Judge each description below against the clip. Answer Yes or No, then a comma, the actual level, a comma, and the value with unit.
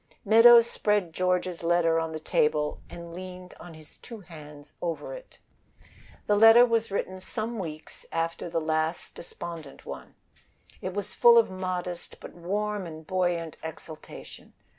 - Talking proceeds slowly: No, average, 145 wpm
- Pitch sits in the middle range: Yes, medium, 180 Hz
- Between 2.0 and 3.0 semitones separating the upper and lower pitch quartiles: No, average, 4.0 semitones